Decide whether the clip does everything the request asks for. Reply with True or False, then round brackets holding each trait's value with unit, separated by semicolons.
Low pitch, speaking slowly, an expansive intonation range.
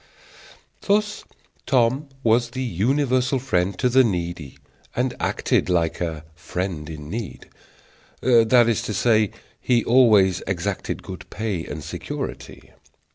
True (110 Hz; 125 wpm; 6.0 semitones)